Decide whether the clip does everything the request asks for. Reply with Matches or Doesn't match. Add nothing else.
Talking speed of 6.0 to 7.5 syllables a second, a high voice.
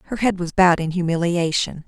Doesn't match